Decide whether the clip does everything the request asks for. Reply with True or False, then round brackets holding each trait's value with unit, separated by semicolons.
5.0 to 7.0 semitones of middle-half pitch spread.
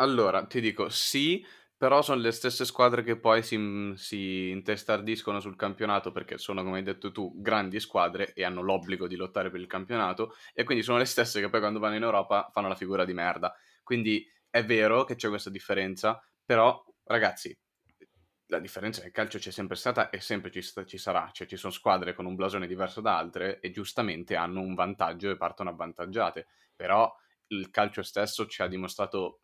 False (2.8 semitones)